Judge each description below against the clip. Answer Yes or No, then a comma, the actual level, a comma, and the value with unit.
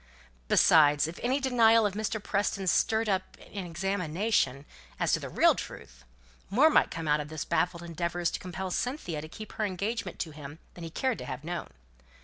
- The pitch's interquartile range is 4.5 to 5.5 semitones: Yes, average, 5.2 semitones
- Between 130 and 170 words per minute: No, average, 195 wpm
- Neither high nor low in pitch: Yes, medium, 180 Hz